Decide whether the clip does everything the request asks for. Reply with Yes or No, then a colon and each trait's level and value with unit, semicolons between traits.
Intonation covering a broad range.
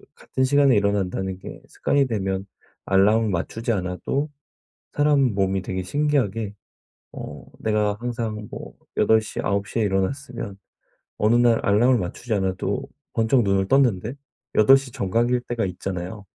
No: average, 4.1 semitones